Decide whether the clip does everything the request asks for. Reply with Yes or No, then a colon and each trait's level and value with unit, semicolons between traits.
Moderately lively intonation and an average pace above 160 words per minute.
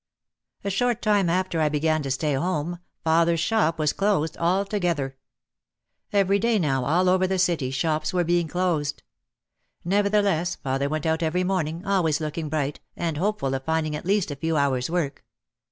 Yes: average, 3.6 semitones; average, 170 wpm